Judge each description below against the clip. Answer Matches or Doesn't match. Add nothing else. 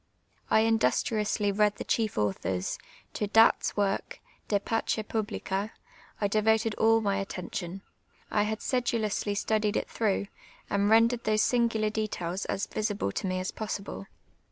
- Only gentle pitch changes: Matches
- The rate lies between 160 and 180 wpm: Doesn't match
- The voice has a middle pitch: Doesn't match